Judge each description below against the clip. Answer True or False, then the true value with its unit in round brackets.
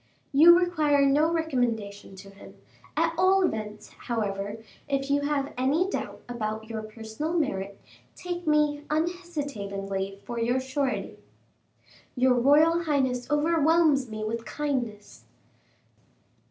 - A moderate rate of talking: False (115 wpm)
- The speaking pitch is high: True (275 Hz)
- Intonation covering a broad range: True (6.0 semitones)